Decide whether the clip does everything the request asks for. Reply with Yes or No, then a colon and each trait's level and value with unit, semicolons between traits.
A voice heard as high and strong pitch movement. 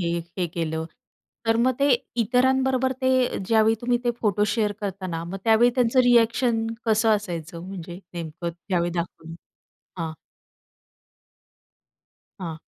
Yes: high, 210 Hz; wide, 5.8 semitones